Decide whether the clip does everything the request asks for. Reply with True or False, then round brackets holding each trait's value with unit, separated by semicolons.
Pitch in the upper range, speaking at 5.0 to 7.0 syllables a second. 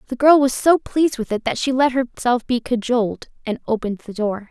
True (245 Hz; 5.6 syllables/s)